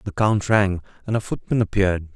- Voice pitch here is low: Yes, low, 100 Hz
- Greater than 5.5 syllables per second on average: Yes, 5.9 syllables/s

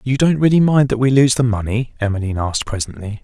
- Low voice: Yes, low, 120 Hz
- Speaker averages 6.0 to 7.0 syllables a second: Yes, 6.5 syllables/s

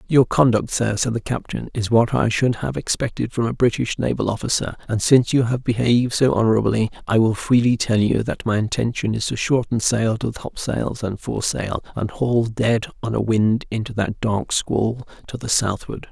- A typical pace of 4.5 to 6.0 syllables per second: Yes, 5.1 syllables/s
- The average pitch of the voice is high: No, low, 115 Hz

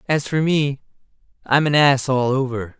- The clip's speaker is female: No, male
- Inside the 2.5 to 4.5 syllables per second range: Yes, 4.4 syllables/s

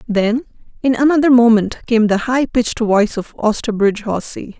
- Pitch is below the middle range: No, high, 230 Hz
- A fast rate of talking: No, average, 155 wpm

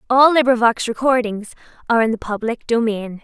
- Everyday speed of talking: Yes, average, 150 wpm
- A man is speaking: No, female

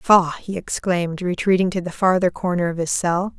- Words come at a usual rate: Yes, average, 195 wpm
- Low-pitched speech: No, medium, 180 Hz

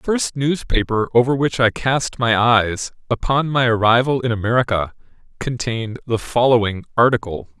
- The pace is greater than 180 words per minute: No, average, 140 wpm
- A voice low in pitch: Yes, low, 120 Hz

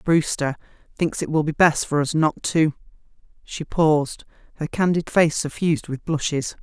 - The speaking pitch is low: No, medium, 155 Hz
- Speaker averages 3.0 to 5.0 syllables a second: Yes, 4.8 syllables/s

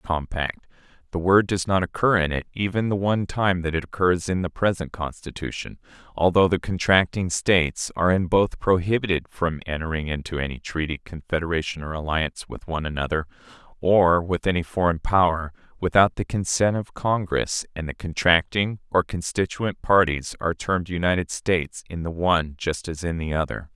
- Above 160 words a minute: Yes, average, 170 wpm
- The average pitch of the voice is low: Yes, very low, 85 Hz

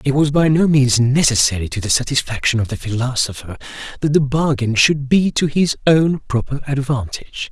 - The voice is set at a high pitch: No, low, 135 Hz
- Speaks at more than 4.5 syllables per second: Yes, 5.3 syllables/s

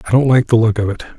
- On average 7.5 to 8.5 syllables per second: Yes, 7.9 syllables/s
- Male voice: Yes, male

